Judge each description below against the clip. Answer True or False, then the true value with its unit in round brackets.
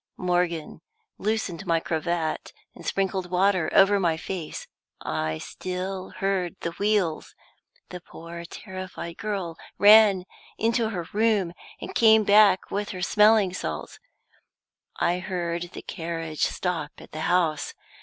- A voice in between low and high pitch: True (180 Hz)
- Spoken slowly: True (125 wpm)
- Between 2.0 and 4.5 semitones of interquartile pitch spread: True (3.1 semitones)